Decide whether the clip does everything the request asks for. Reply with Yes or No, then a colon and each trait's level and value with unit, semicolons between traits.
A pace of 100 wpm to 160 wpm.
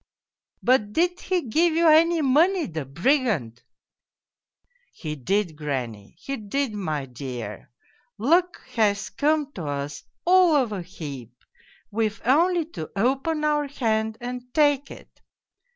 Yes: average, 145 wpm